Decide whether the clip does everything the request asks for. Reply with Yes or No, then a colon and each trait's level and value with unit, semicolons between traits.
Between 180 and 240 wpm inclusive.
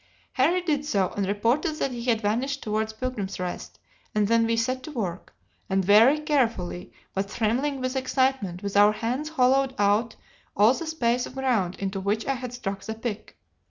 Yes: average, 185 wpm